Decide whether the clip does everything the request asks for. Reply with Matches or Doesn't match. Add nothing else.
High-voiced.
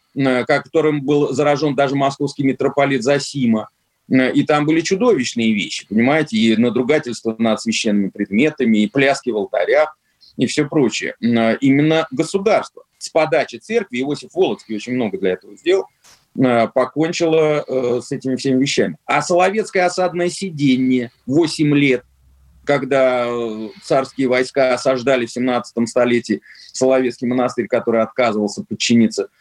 Doesn't match